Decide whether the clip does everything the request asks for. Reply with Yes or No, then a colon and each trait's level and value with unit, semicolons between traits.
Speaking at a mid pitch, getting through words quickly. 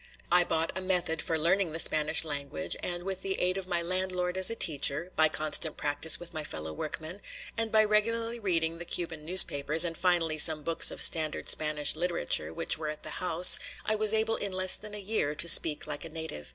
Yes: medium, 170 Hz; fast, 215 wpm